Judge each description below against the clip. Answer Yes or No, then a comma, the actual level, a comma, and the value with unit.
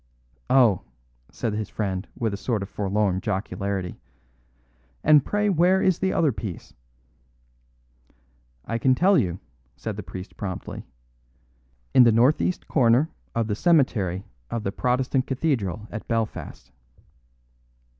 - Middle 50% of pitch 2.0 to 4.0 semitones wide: No, average, 5.2 semitones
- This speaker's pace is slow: Yes, slow, 125 wpm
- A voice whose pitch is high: No, low, 115 Hz